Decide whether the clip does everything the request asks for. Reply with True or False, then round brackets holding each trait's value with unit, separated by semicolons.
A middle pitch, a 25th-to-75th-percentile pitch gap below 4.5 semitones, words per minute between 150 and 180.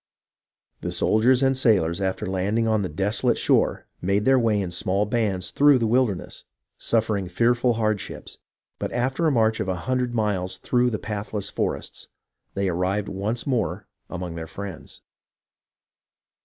False (105 Hz; 4.0 semitones; 155 wpm)